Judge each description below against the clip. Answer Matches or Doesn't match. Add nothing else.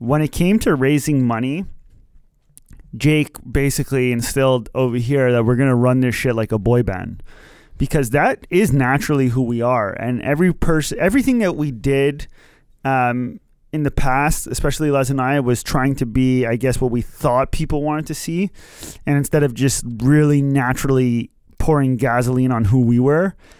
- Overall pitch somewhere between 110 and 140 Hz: Matches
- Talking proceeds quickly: Doesn't match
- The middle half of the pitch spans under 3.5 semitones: Matches